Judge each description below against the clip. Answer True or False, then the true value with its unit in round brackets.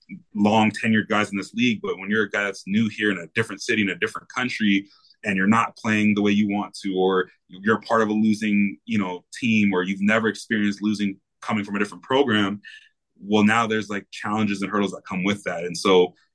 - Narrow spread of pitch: True (1.6 semitones)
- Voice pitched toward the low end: True (105 Hz)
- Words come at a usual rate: False (230 wpm)